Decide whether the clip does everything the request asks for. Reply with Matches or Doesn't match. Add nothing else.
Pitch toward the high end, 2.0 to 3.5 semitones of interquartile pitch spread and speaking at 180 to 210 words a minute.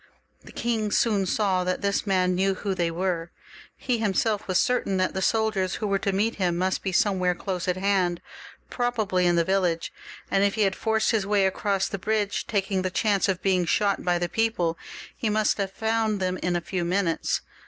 Matches